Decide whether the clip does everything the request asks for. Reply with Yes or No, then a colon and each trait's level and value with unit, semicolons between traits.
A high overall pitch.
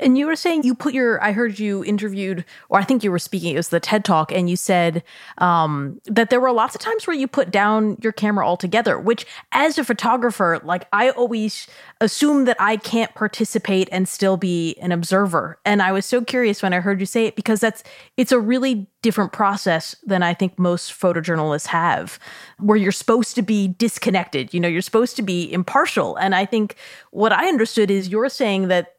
Yes: high, 205 Hz